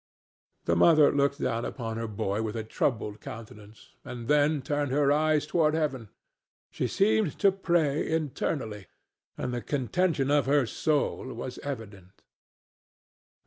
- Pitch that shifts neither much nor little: Yes, average, 5.0 semitones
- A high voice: No, low, 135 Hz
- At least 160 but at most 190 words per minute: No, average, 145 wpm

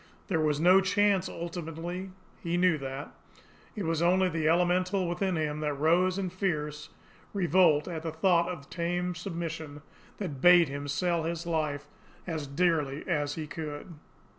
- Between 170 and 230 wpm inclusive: No, average, 155 wpm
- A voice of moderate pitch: Yes, medium, 170 Hz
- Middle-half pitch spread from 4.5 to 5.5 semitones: No, average, 3.0 semitones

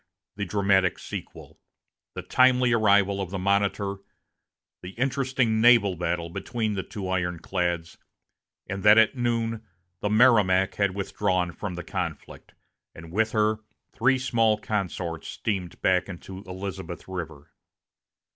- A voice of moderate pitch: No, low, 100 Hz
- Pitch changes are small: No, average, 3.3 semitones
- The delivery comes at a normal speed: No, slow, 125 wpm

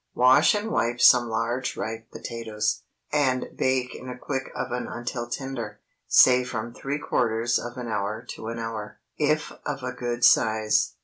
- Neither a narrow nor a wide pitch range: No, narrow, 2.2 semitones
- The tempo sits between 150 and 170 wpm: Yes, average, 165 wpm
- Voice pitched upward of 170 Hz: No, low, 120 Hz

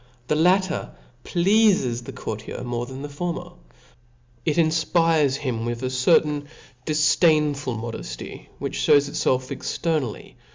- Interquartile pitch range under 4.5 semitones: No, average, 4.8 semitones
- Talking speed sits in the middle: No, slow, 115 wpm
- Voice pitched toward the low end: No, medium, 145 Hz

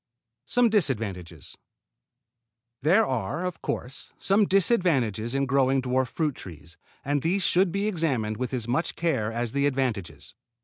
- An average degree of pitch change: No, wide, 7.1 semitones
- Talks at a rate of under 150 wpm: Yes, average, 140 wpm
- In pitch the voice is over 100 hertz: Yes, low, 135 Hz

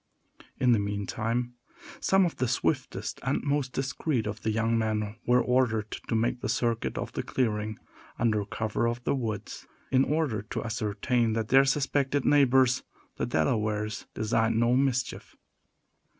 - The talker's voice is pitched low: Yes, low, 115 Hz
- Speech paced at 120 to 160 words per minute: Yes, average, 150 wpm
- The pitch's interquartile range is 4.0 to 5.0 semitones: No, average, 3.1 semitones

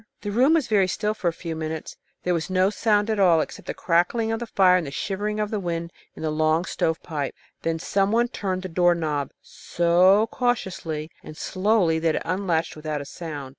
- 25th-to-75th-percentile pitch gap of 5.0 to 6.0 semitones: No, average, 4.3 semitones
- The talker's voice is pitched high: No, medium, 180 Hz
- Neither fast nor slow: No, fast, 210 wpm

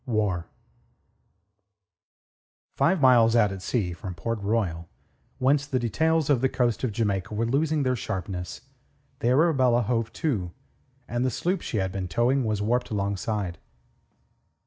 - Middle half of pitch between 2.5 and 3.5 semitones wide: No, average, 4.7 semitones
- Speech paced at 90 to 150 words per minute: Yes, average, 145 wpm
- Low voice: Yes, low, 115 Hz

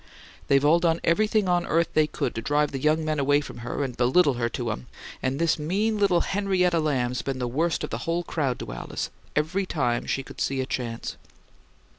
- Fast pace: Yes, fast, 215 wpm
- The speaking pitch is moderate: Yes, medium, 150 Hz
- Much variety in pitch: No, average, 4.7 semitones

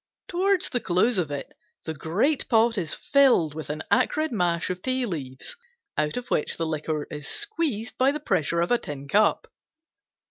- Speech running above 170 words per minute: Yes, average, 180 wpm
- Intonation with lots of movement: Yes, wide, 8.7 semitones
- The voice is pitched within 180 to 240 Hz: Yes, medium, 185 Hz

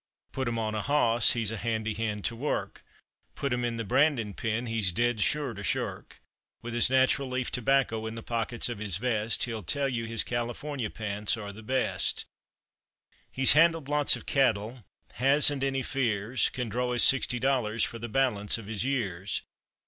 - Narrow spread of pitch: No, average, 3.2 semitones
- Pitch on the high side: No, low, 120 Hz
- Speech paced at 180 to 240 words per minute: Yes, average, 185 wpm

